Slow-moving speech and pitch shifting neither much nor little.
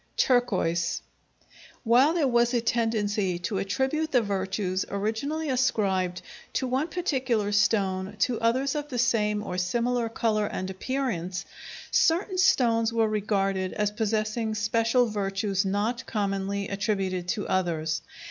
Yes: slow, 130 wpm; average, 3.9 semitones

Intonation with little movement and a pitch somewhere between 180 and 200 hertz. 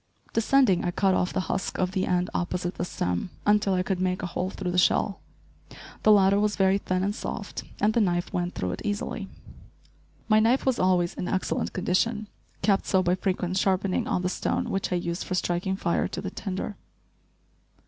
Yes: narrow, 2.1 semitones; medium, 185 Hz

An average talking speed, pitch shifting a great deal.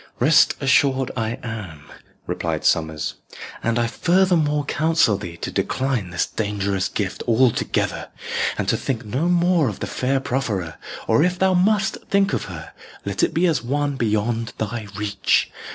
Yes: average, 165 wpm; wide, 6.7 semitones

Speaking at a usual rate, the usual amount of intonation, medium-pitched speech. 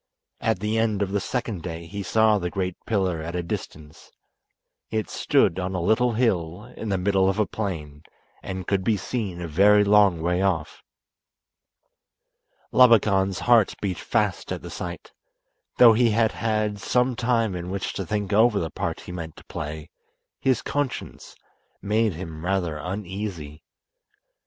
No: average, 160 wpm; average, 3.7 semitones; low, 100 Hz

